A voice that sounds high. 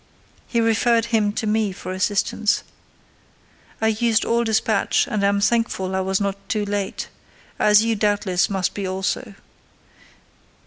Yes: high, 210 Hz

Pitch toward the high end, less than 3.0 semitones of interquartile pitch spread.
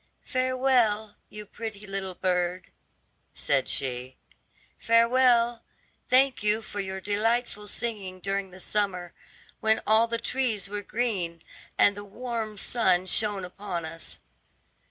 No: high, 210 Hz; average, 3.6 semitones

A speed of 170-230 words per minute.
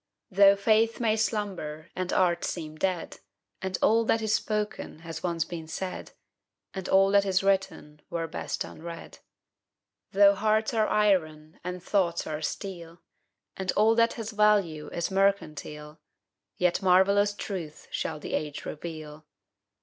No: average, 140 wpm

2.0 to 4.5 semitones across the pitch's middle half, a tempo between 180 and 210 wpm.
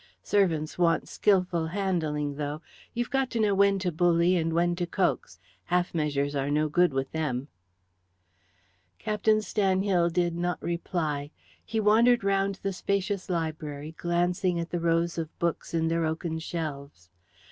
No: average, 3.5 semitones; average, 150 wpm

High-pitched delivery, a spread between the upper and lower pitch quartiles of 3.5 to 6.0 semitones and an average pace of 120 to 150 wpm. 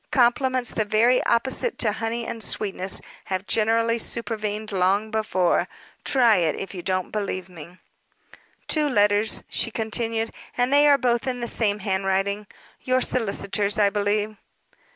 No: high, 215 Hz; average, 2.8 semitones; average, 145 wpm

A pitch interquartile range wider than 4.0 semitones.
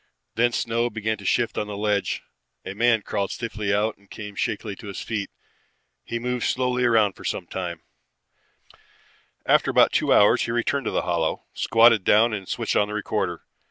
No: average, 2.7 semitones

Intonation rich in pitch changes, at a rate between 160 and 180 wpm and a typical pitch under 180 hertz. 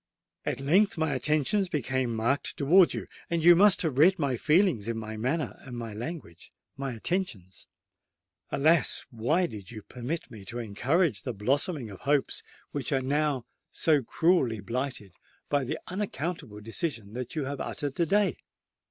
No: wide, 6.0 semitones; average, 150 wpm; medium, 140 Hz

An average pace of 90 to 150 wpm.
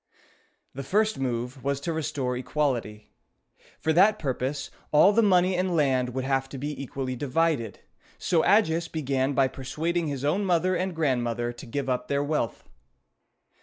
No: average, 160 wpm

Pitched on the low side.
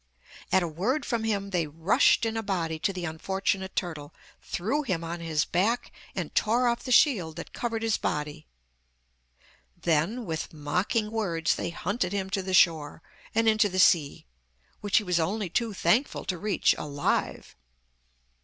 No: high, 190 Hz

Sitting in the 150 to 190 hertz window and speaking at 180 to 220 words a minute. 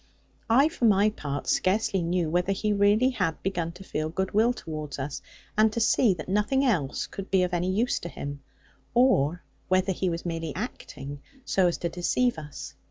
Yes: medium, 185 Hz; average, 185 wpm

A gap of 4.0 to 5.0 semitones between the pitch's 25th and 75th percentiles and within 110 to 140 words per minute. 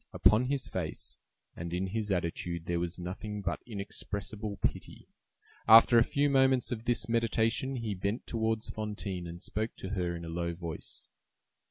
No: average, 4.6 semitones; average, 165 wpm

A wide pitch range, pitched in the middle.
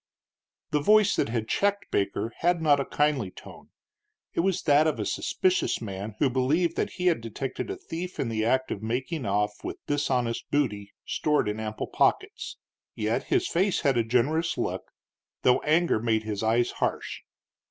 No: wide, 6.9 semitones; low, 130 Hz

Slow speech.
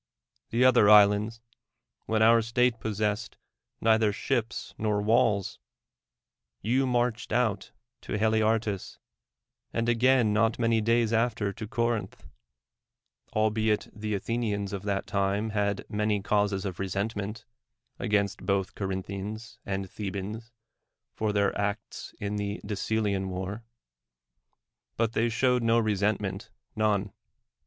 Yes: slow, 115 wpm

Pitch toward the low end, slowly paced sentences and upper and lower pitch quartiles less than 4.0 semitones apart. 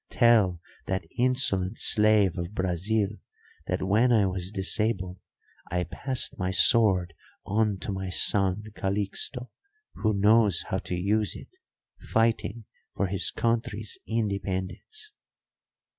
Yes: low, 100 Hz; slow, 115 wpm; average, 3.1 semitones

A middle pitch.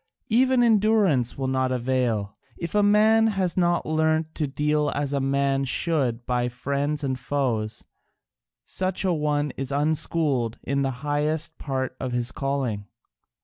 Yes: medium, 145 Hz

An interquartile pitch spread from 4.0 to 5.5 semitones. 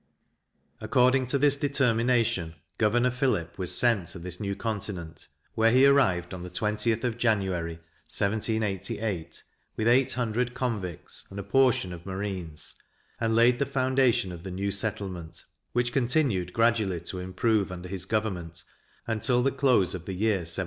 Yes: average, 4.9 semitones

